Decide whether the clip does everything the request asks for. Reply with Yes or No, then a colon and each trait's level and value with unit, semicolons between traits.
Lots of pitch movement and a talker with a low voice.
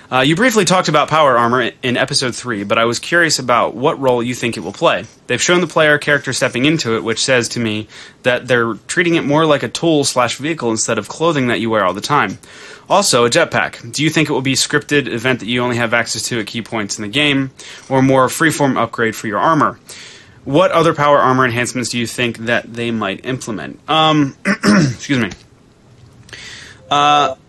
No: average, 4.0 semitones; low, 130 Hz